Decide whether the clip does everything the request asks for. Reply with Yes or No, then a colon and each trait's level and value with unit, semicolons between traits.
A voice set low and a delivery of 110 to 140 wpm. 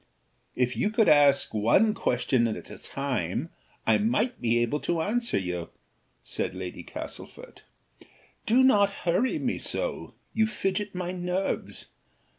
No: medium, 175 Hz; slow, 135 wpm